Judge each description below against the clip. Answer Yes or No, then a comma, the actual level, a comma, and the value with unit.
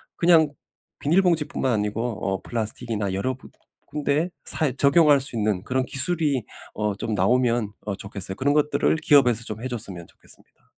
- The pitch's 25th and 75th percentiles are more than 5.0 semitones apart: Yes, wide, 5.6 semitones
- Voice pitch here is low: Yes, low, 125 Hz